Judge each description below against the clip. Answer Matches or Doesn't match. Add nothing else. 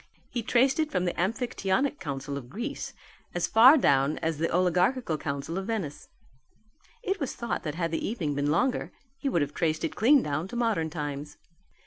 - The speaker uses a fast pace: Doesn't match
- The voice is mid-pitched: Matches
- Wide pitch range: Matches